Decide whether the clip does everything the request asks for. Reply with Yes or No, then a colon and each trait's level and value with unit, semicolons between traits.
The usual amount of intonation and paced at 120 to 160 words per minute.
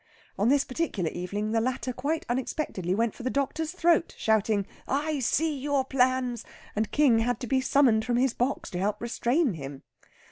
No: average, 4.3 semitones; average, 180 wpm